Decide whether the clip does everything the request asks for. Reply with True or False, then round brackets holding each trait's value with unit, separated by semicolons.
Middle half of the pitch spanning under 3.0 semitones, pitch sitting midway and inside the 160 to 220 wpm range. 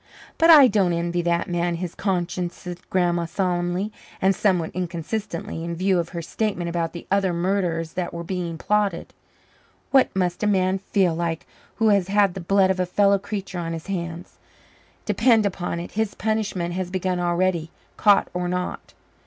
True (2.4 semitones; 180 Hz; 170 wpm)